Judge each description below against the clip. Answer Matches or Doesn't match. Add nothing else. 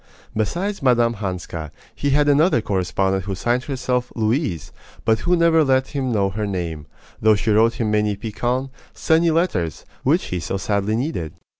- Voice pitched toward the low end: Matches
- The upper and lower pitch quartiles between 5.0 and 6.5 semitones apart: Matches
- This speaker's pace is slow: Doesn't match